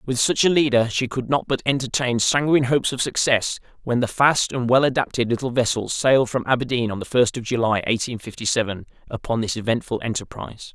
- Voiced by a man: Yes, male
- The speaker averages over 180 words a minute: Yes, average, 200 wpm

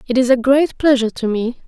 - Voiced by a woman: Yes, female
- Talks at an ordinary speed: No, fast, 250 wpm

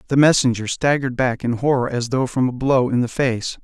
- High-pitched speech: No, low, 125 Hz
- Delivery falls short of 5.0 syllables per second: No, 5.6 syllables/s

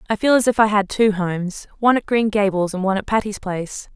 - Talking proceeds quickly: Yes, fast, 245 wpm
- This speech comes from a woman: Yes, female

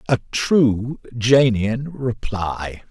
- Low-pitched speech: Yes, low, 120 Hz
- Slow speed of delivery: Yes, slow, 85 wpm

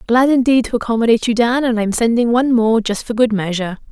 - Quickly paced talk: Yes, fast, 230 wpm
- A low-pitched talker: No, high, 230 Hz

